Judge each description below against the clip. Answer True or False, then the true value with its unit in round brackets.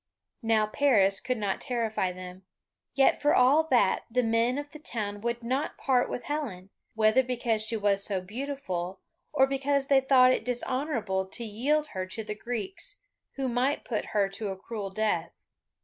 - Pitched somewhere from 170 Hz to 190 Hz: False (235 Hz)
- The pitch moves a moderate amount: True (4.7 semitones)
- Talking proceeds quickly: False (175 wpm)